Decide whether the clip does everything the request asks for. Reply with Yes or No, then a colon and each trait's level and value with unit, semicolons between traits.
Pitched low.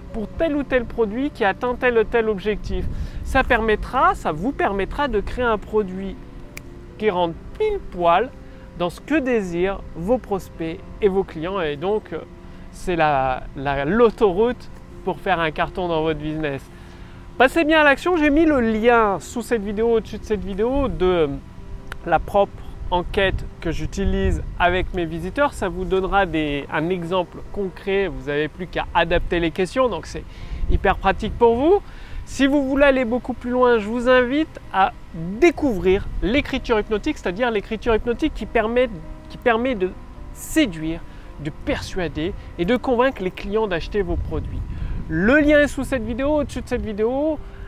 No: high, 210 Hz